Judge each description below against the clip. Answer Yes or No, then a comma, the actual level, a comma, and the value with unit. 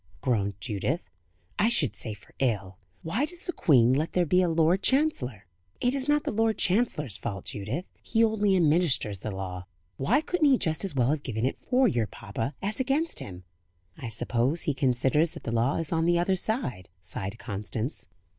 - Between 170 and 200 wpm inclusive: Yes, average, 195 wpm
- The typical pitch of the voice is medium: Yes, medium, 150 Hz